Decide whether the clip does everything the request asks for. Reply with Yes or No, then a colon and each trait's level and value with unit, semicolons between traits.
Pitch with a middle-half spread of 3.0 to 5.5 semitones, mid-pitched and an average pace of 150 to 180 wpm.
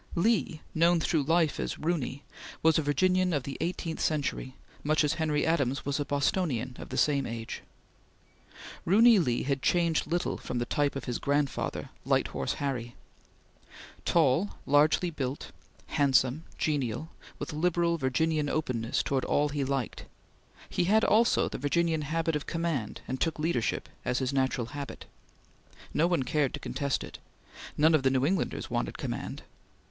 Yes: average, 3.7 semitones; medium, 150 Hz; average, 160 wpm